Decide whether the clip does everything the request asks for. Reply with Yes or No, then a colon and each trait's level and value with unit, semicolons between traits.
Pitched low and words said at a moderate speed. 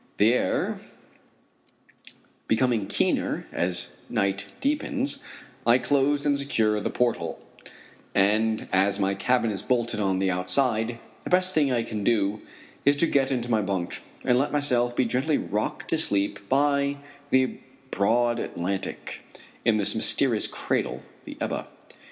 Yes: low, 115 Hz; average, 145 wpm